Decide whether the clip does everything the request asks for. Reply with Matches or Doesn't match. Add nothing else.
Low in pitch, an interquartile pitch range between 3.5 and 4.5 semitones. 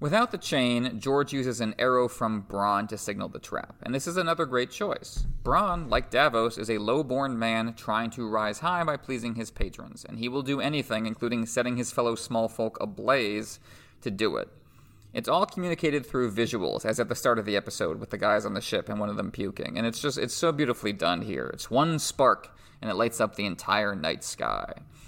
Matches